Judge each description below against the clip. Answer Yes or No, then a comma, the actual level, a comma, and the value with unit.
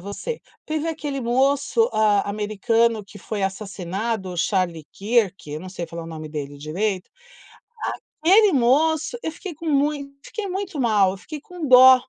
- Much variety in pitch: Yes, wide, 7.5 semitones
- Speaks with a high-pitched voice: Yes, high, 225 Hz